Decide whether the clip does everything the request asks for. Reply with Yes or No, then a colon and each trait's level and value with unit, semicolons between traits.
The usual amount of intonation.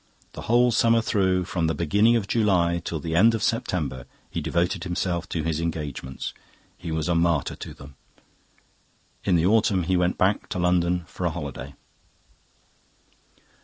Yes: average, 3.2 semitones